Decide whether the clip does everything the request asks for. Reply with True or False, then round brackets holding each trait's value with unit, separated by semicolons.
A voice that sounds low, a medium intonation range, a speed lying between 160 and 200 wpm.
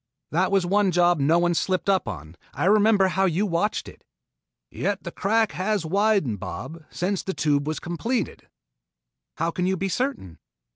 False (185 Hz; 3.5 semitones; 180 wpm)